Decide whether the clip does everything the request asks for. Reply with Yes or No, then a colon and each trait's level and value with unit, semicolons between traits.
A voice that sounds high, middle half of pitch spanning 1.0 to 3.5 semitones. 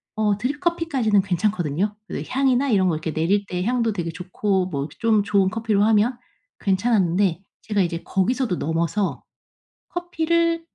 No: high, 205 Hz; average, 5.1 semitones